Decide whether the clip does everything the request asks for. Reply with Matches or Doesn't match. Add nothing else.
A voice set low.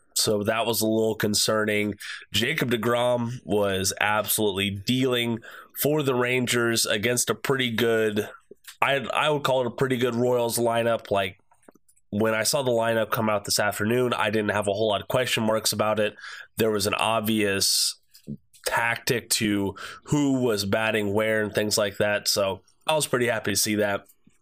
Matches